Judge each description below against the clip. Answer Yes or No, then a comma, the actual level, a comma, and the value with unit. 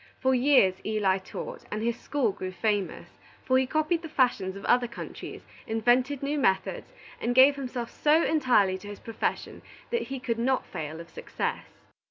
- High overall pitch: Yes, high, 245 Hz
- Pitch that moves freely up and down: No, average, 4.8 semitones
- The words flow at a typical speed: Yes, average, 175 wpm